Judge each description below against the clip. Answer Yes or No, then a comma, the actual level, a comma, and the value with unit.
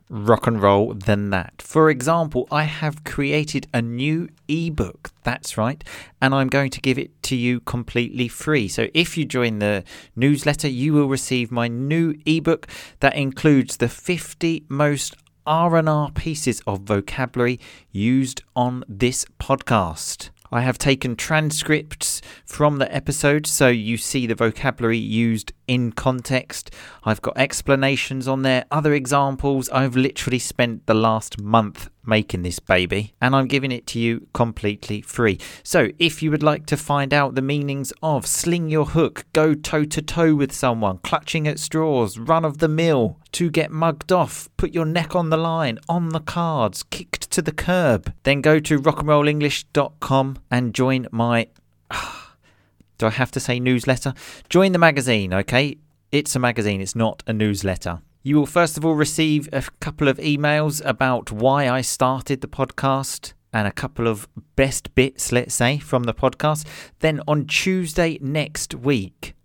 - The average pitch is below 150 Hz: Yes, low, 135 Hz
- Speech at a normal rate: Yes, average, 165 wpm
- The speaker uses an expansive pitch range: No, average, 4.5 semitones